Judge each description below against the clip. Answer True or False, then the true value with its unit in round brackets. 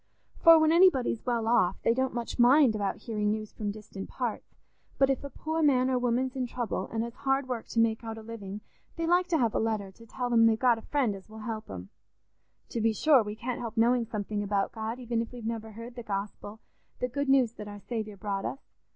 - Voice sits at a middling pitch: False (230 Hz)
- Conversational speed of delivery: False (235 wpm)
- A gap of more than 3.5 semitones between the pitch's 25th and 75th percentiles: False (2.8 semitones)